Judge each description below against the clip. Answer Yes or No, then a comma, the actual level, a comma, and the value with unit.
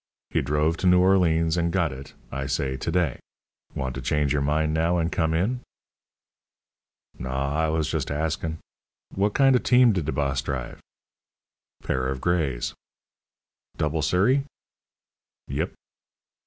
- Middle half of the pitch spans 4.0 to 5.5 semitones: Yes, average, 4.3 semitones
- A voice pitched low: Yes, very low, 80 Hz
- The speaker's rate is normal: Yes, average, 145 wpm